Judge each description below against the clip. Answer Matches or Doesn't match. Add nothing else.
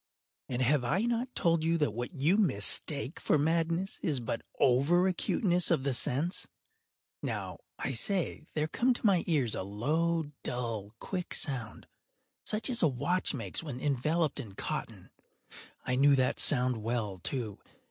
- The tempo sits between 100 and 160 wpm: Matches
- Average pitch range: Doesn't match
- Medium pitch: Matches